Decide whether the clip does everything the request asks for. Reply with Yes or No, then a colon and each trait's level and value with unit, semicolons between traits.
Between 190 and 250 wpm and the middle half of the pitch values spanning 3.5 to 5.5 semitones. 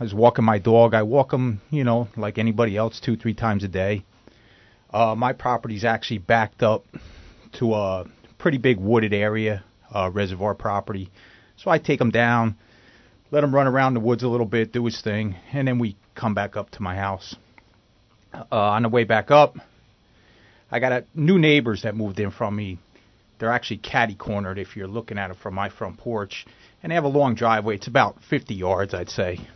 No: fast, 205 wpm; average, 2.9 semitones